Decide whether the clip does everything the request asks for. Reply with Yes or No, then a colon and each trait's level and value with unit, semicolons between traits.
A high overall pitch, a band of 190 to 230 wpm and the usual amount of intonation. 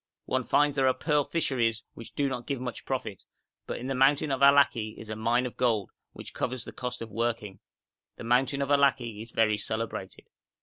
No: low, 125 Hz; average, 200 wpm; average, 3.3 semitones